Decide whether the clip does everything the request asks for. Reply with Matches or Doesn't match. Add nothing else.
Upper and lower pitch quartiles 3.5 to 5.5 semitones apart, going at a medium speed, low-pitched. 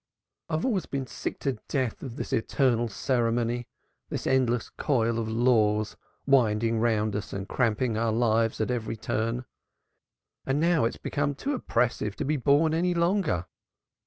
Matches